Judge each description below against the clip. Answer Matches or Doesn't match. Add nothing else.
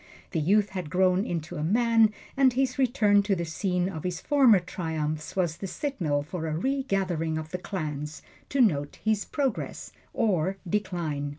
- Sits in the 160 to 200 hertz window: Matches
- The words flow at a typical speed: Matches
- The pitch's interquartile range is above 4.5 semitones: Matches